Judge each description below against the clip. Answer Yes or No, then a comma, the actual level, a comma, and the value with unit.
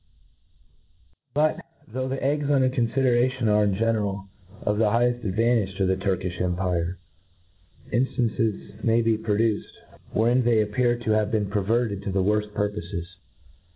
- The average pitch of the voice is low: Yes, low, 110 Hz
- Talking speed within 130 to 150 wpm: Yes, average, 145 wpm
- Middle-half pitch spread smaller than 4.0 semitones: Yes, average, 3.2 semitones